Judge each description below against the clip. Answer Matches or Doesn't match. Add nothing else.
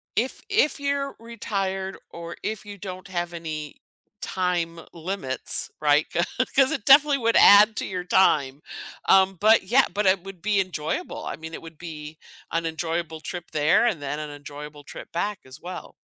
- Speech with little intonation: Doesn't match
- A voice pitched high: Doesn't match